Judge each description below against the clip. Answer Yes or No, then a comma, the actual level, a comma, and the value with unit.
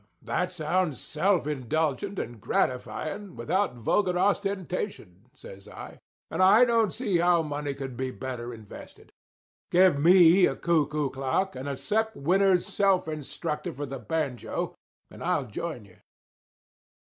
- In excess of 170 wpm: No, slow, 135 wpm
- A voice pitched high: No, medium, 155 Hz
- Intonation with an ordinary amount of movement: No, wide, 6.1 semitones